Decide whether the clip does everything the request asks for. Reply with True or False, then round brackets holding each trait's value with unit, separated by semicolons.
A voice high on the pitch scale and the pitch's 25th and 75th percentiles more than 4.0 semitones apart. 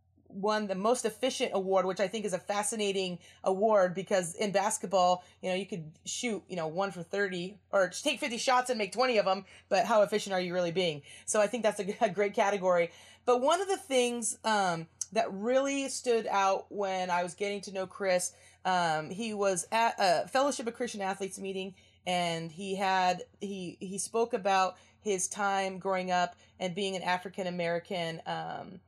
False (195 Hz; 3.3 semitones)